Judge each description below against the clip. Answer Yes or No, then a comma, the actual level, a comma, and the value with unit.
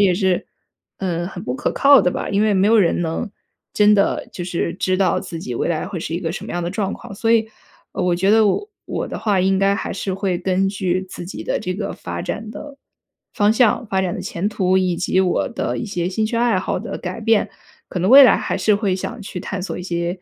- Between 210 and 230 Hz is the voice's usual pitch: No, high, 190 Hz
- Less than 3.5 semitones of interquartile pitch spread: Yes, average, 2.8 semitones